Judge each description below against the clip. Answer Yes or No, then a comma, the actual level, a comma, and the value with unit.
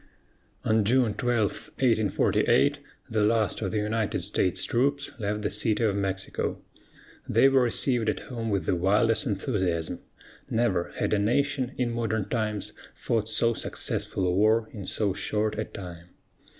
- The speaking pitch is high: No, low, 110 Hz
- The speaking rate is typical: Yes, average, 150 wpm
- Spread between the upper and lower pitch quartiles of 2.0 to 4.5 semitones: Yes, narrow, 2.6 semitones